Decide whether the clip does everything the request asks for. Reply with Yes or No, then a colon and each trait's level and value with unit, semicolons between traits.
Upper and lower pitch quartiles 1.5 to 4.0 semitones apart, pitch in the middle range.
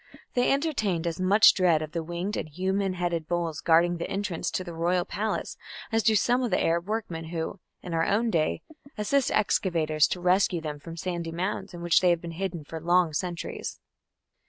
Yes: average, 2.9 semitones; medium, 175 Hz